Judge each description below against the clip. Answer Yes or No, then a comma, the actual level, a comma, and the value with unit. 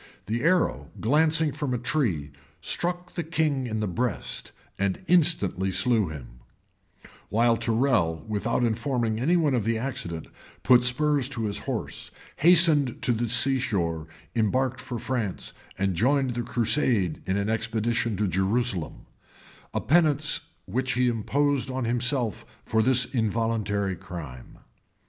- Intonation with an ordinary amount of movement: Yes, average, 4.7 semitones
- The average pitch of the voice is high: No, low, 120 Hz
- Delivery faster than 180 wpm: No, average, 140 wpm